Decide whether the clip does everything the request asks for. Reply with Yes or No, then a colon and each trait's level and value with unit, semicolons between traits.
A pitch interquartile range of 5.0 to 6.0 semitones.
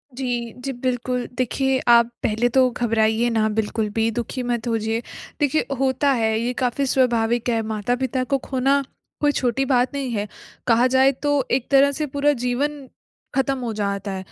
No: average, 2.9 semitones